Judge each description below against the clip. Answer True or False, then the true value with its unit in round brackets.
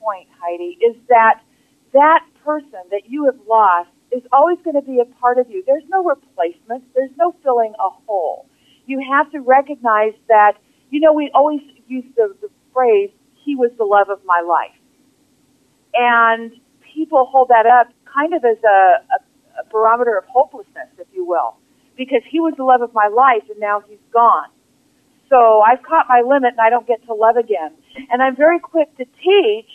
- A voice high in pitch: True (260 Hz)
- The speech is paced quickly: False (190 wpm)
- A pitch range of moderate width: True (4.2 semitones)